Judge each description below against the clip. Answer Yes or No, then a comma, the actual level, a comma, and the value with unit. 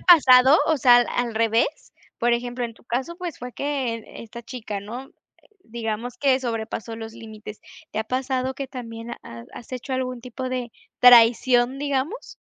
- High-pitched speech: Yes, high, 245 Hz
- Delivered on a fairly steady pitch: Yes, narrow, 2.3 semitones